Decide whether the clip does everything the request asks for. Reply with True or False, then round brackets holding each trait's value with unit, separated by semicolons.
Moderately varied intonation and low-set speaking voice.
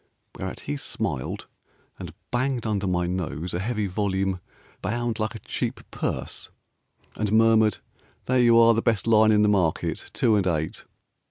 True (3.5 semitones; 105 Hz)